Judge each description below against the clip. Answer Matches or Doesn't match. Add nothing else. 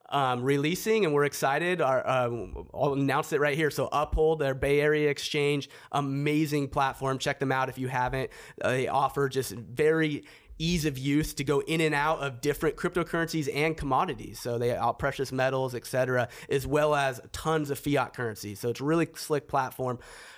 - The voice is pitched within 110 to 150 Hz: Matches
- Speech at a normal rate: Matches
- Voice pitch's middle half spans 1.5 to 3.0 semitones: Matches